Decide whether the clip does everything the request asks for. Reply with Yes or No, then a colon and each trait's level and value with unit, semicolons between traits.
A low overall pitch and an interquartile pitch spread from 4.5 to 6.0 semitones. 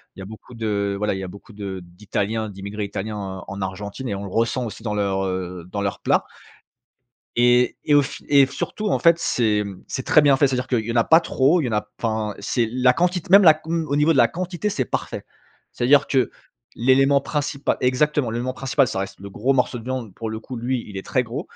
Yes: low, 120 Hz; average, 5.1 semitones